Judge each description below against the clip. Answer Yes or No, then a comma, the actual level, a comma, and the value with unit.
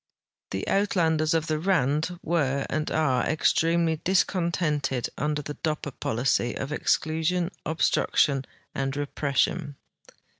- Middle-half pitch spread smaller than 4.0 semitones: Yes, average, 3.1 semitones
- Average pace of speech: No, slow, 115 wpm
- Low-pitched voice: No, medium, 155 Hz